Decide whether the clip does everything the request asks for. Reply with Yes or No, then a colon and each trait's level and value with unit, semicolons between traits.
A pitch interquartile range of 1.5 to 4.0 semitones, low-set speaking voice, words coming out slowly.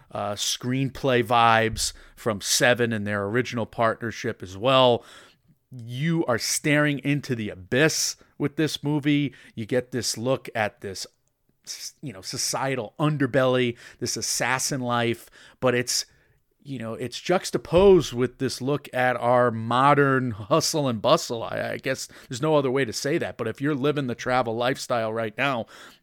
No: average, 3.4 semitones; low, 125 Hz; average, 155 wpm